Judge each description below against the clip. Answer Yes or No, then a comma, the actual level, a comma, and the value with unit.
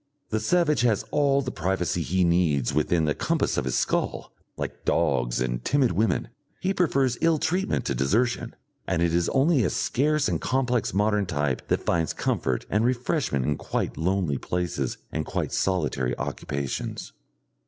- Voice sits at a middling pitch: No, very low, 95 Hz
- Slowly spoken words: No, average, 165 wpm